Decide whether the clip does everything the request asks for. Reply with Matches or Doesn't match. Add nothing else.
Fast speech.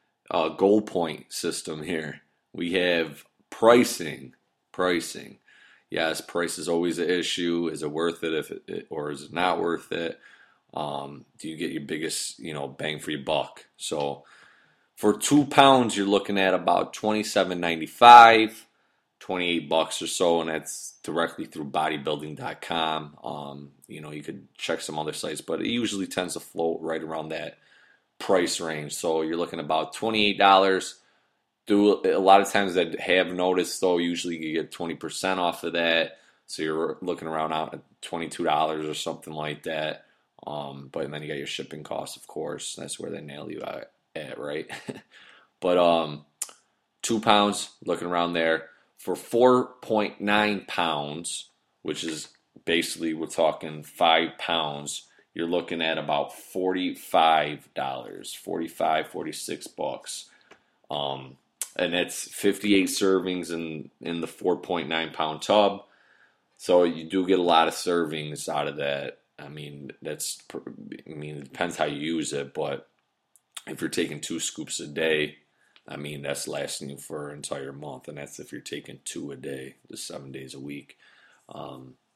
Doesn't match